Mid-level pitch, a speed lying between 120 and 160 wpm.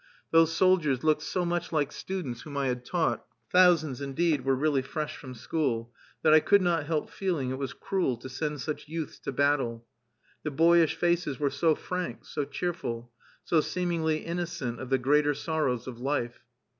No: medium, 150 Hz; average, 180 wpm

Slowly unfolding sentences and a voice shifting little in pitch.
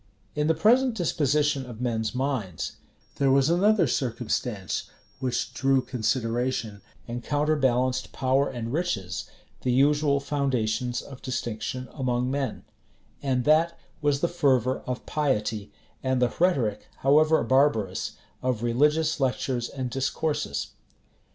No: slow, 120 wpm; average, 3.3 semitones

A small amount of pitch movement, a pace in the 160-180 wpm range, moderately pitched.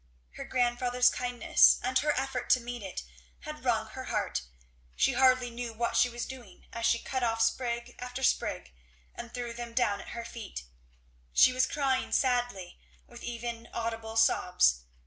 No: narrow, 1.4 semitones; average, 165 wpm; high, 240 Hz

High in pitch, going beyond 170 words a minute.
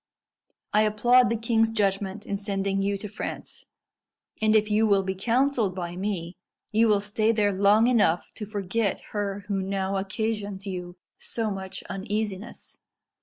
No: high, 205 Hz; average, 155 wpm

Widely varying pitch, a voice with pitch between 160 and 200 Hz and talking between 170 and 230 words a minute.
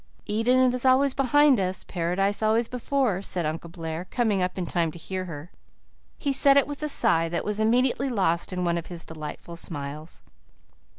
Yes: wide, 6.8 semitones; high, 190 Hz; average, 185 wpm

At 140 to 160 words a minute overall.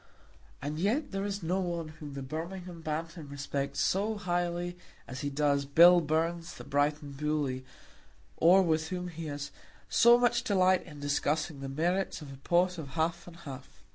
No: average, 170 wpm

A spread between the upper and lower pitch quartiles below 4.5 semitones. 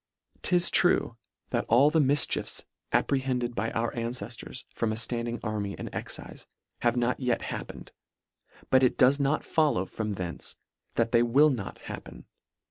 Yes: average, 2.9 semitones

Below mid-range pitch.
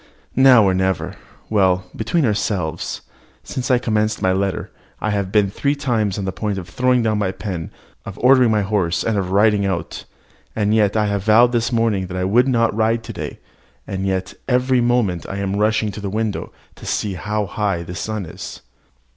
Yes: low, 105 Hz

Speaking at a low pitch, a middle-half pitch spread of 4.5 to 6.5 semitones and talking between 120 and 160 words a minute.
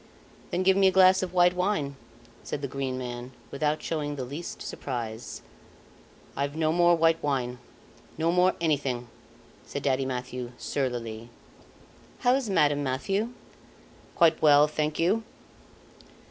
No: medium, 150 Hz; average, 5.2 semitones; slow, 135 wpm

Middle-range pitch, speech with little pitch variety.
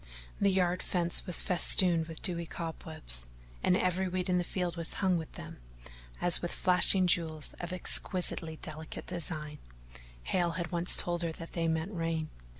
Yes: medium, 175 Hz; narrow, 1.9 semitones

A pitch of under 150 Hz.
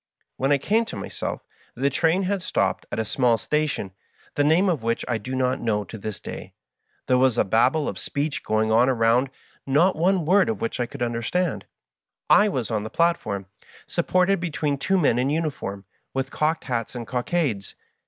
Yes: low, 135 Hz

